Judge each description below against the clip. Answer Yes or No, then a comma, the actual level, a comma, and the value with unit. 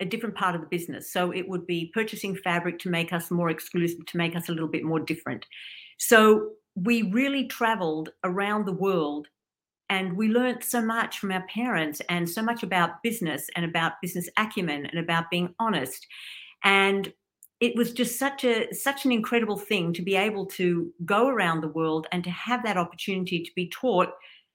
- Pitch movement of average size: Yes, average, 4.5 semitones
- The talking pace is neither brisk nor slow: Yes, average, 195 wpm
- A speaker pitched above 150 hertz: Yes, medium, 185 Hz